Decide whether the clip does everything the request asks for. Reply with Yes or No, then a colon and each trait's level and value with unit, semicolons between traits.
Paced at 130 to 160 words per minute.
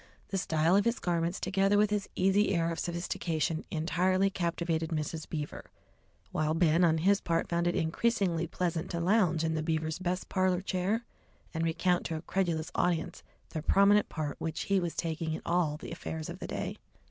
No: average, 185 wpm